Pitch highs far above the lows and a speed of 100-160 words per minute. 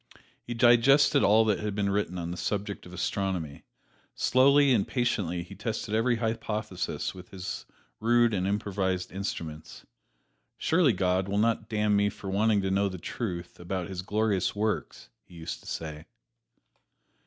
No: average, 3.4 semitones; average, 155 wpm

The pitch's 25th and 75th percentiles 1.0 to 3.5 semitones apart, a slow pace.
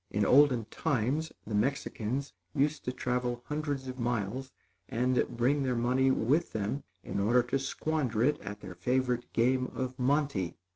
No: average, 2.8 semitones; average, 155 wpm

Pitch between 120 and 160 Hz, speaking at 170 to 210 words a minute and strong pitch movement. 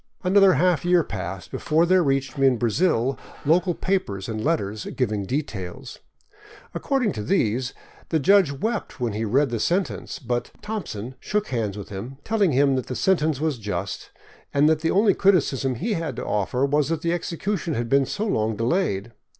Yes: medium, 140 Hz; average, 180 wpm; wide, 7.5 semitones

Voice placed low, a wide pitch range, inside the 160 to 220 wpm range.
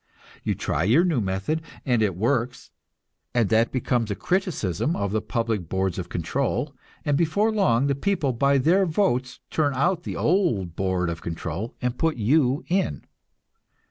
Yes: low, 125 Hz; wide, 7.6 semitones; average, 165 wpm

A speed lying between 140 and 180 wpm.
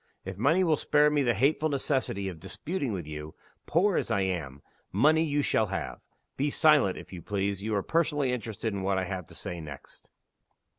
No: average, 200 wpm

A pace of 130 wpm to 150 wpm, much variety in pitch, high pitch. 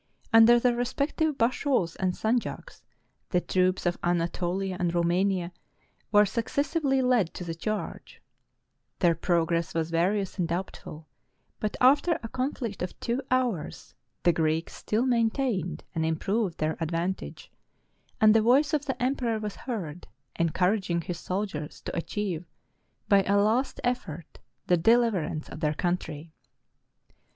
Yes: slow, 135 wpm; wide, 5.8 semitones; high, 195 Hz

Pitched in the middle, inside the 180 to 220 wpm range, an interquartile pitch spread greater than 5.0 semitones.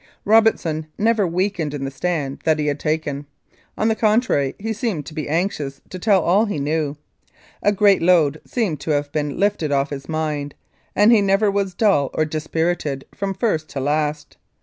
Yes: medium, 160 Hz; average, 185 wpm; wide, 5.4 semitones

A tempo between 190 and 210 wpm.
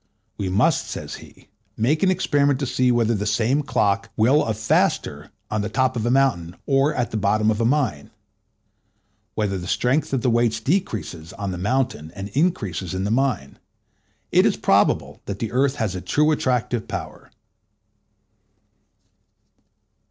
No: average, 165 wpm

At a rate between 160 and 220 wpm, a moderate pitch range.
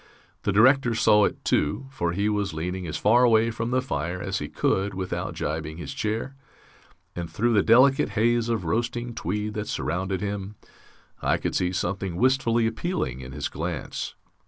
Yes: average, 175 wpm; average, 4.7 semitones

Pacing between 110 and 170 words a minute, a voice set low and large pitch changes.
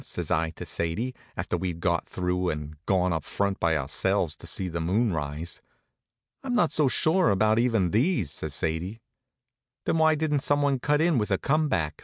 No: average, 190 wpm; very low, 95 Hz; wide, 8.8 semitones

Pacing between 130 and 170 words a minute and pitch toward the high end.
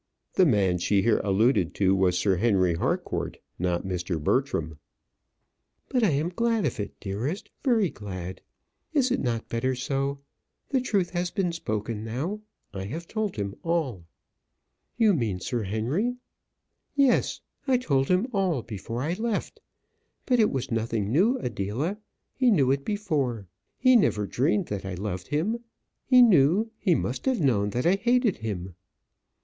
No: average, 155 wpm; low, 135 Hz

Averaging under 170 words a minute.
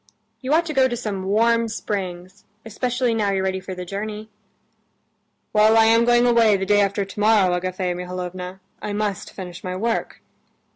No: average, 175 wpm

